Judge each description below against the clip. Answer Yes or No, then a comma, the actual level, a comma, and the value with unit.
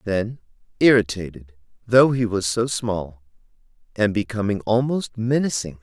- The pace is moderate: No, slow, 115 wpm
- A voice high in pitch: No, low, 110 Hz